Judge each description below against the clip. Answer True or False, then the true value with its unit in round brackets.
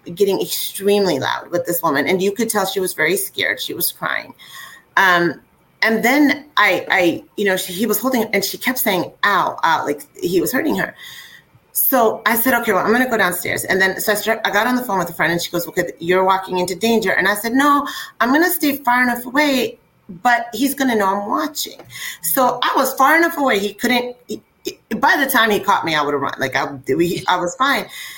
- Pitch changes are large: True (5.8 semitones)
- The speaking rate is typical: False (235 wpm)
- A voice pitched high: True (225 Hz)